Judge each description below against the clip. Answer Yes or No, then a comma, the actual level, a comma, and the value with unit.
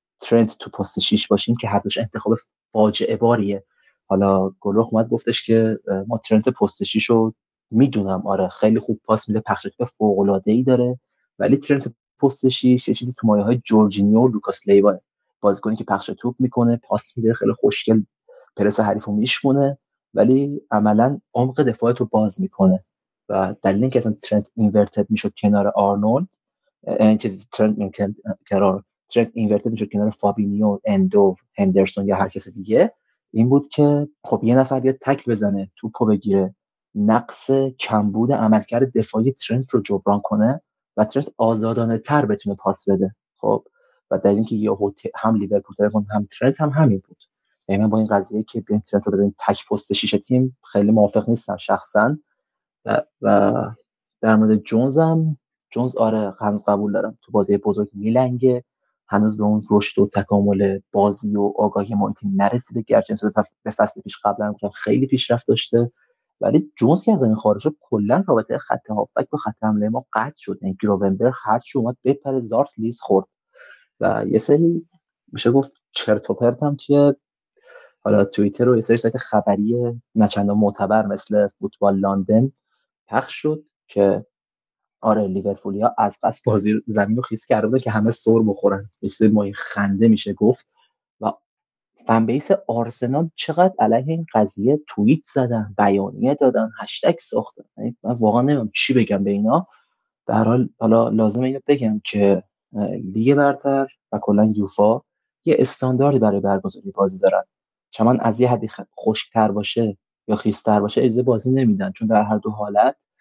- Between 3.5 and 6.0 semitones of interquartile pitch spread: Yes, average, 3.9 semitones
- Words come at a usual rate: No, fast, 160 wpm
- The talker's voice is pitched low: Yes, low, 110 Hz